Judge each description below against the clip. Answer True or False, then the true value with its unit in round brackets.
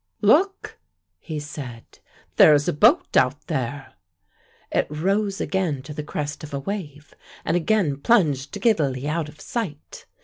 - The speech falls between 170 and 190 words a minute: False (145 wpm)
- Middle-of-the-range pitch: True (150 Hz)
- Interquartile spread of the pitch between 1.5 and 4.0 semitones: False (5.4 semitones)